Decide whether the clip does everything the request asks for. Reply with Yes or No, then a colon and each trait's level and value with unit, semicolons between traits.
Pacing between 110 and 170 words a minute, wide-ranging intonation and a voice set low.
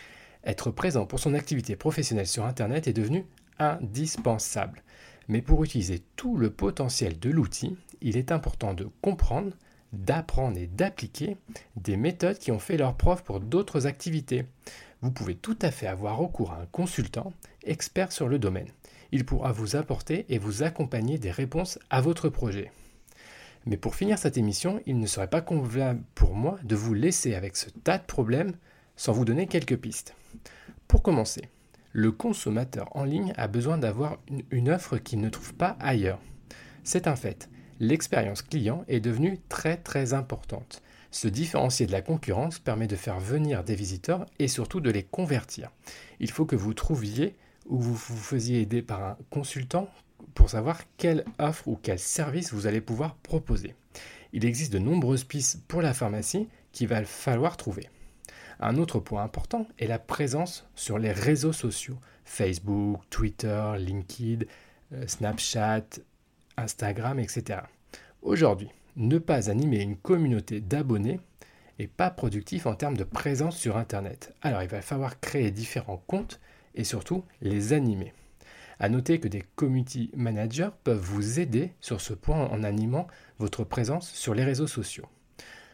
Yes: average, 160 wpm; wide, 5.9 semitones; low, 125 Hz